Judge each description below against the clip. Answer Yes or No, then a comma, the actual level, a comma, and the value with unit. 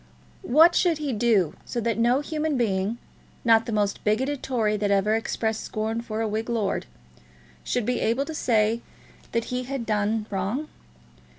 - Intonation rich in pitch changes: No, average, 2.9 semitones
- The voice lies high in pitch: Yes, high, 230 Hz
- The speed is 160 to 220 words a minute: Yes, average, 170 wpm